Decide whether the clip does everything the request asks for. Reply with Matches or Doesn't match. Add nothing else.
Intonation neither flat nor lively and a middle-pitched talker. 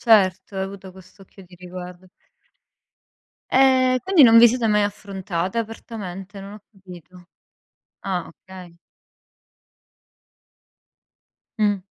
Doesn't match